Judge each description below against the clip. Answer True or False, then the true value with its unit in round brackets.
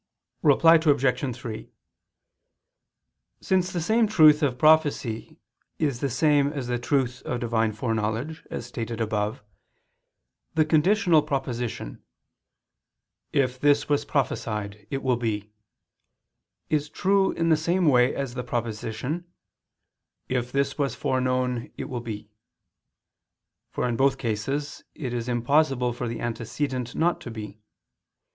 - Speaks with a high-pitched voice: False (130 Hz)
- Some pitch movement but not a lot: True (4.2 semitones)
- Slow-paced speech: True (125 wpm)